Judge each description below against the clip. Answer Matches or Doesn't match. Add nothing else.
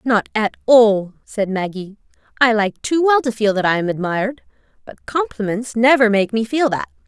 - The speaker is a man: Doesn't match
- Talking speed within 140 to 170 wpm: Doesn't match